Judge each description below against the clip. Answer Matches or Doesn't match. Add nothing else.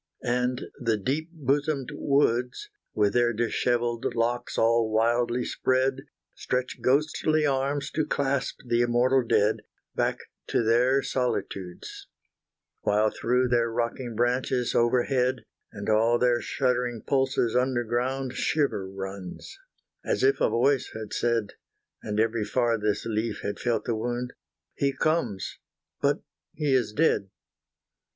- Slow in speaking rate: Matches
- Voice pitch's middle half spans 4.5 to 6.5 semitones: Doesn't match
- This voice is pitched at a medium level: Doesn't match